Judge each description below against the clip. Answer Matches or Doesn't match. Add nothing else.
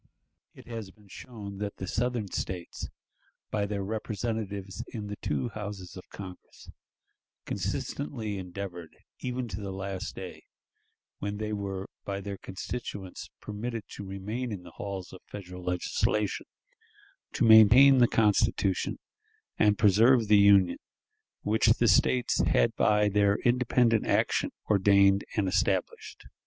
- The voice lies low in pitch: Matches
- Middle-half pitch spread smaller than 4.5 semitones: Matches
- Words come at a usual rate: Doesn't match